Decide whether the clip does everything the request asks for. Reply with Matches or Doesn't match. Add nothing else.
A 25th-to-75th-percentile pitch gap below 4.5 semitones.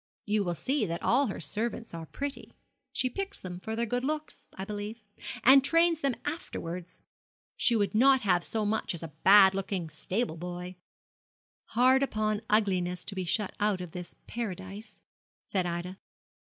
Doesn't match